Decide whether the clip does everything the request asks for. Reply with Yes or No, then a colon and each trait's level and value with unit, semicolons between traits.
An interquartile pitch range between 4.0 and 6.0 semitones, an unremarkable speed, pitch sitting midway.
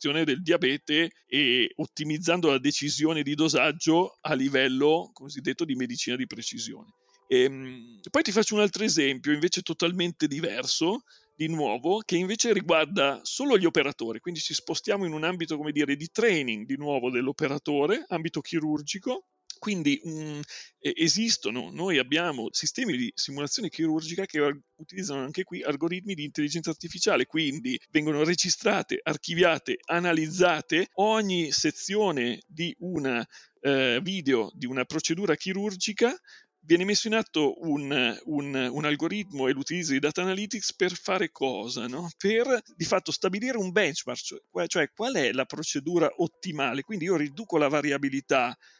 Yes: average, 4.9 semitones; average, 145 wpm; medium, 165 Hz